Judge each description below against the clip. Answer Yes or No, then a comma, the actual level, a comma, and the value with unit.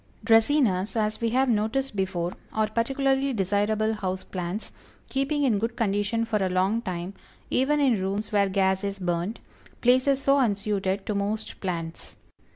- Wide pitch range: No, average, 3.9 semitones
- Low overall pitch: No, high, 210 Hz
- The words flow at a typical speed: Yes, average, 155 wpm